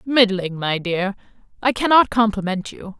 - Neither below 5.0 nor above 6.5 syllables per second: No, 4.5 syllables/s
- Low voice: No, high, 210 Hz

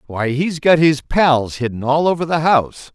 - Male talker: Yes, male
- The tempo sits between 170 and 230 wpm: Yes, fast, 205 wpm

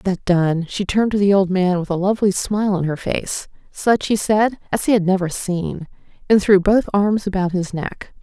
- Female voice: Yes, female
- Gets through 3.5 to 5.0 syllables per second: Yes, 4.9 syllables/s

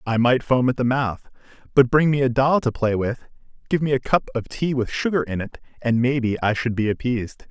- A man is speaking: Yes, male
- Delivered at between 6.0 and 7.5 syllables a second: No, 5.5 syllables/s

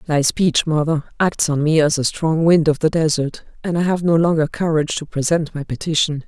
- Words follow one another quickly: Yes, fast, 220 wpm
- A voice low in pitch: No, medium, 155 Hz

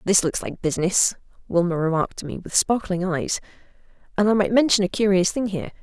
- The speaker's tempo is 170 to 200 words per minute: Yes, average, 195 wpm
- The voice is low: No, high, 190 Hz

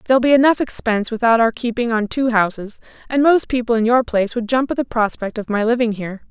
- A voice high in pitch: Yes, high, 235 Hz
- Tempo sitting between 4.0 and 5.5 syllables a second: No, 6.4 syllables/s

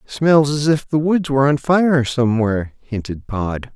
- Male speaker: Yes, male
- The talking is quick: No, average, 175 wpm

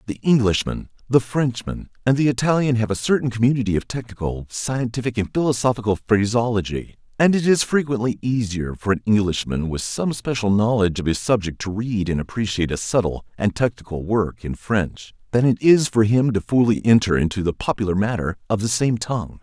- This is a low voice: Yes, low, 110 Hz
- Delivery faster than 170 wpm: Yes, average, 180 wpm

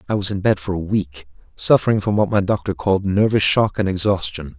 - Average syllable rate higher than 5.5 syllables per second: Yes, 5.8 syllables/s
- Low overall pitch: Yes, low, 100 Hz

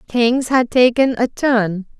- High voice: Yes, high, 240 Hz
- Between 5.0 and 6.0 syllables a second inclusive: No, 3.6 syllables/s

